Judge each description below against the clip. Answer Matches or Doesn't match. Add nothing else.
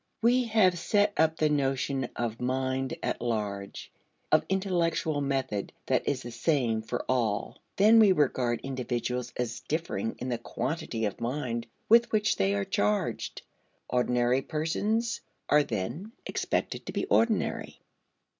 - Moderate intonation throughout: Doesn't match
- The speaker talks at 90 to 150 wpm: Matches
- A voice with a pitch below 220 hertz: Matches